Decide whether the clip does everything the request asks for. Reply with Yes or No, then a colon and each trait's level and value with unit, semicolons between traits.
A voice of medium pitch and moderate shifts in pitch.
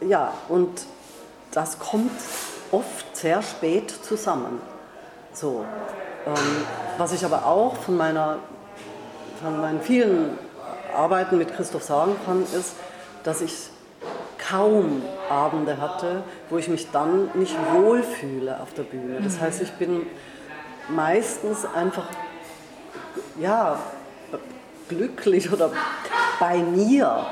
No: medium, 180 Hz; wide, 6.4 semitones